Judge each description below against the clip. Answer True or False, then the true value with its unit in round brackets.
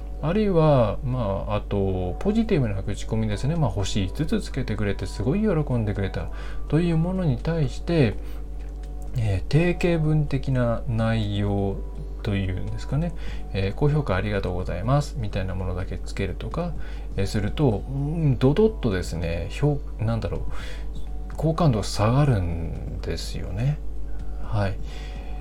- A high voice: False (115 Hz)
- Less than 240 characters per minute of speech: False (300 characters per minute)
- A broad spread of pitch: True (7.0 semitones)